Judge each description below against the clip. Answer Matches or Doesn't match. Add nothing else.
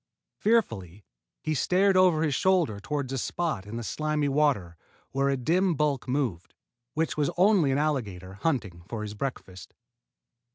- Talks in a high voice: Doesn't match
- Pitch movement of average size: Doesn't match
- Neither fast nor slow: Matches